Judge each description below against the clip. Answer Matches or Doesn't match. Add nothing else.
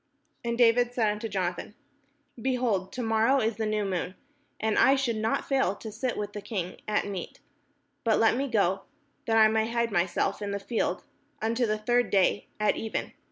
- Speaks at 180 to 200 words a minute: Matches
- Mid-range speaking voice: Doesn't match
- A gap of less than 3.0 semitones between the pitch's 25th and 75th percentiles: Matches